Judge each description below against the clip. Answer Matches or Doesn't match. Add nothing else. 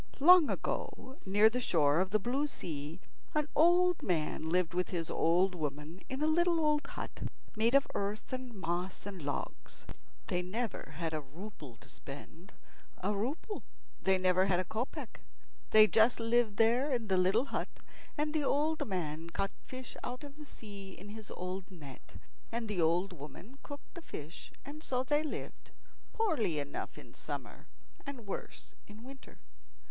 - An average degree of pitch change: Doesn't match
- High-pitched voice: Matches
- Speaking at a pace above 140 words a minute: Matches